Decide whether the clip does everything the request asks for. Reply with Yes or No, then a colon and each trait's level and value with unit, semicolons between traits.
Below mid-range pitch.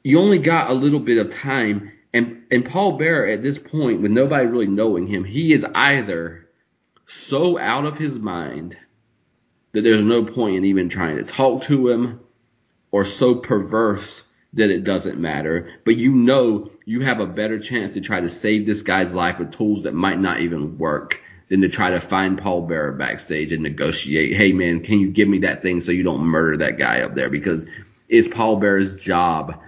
Yes: low, 105 Hz